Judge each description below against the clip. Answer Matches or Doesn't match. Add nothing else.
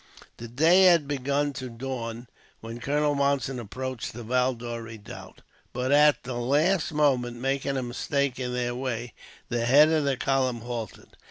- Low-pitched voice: Matches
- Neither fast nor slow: Matches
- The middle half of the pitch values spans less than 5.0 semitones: Matches